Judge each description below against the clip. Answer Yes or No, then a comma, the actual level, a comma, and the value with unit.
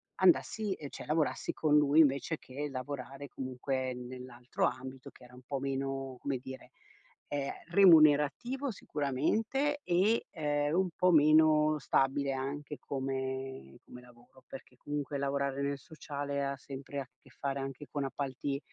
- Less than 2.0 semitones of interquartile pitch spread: No, narrow, 2.4 semitones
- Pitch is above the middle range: No, medium, 140 Hz